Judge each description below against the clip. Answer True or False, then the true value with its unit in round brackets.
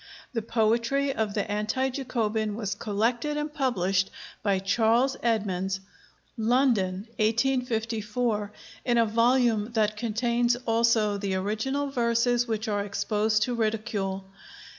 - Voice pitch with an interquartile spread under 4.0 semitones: True (2.6 semitones)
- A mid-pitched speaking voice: False (225 Hz)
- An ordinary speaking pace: False (120 wpm)